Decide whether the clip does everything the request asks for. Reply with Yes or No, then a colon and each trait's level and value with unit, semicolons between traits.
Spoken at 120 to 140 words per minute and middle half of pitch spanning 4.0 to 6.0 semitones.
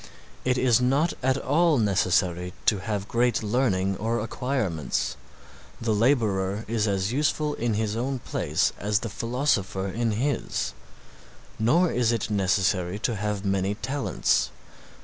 Yes: slow, 135 wpm; average, 4.3 semitones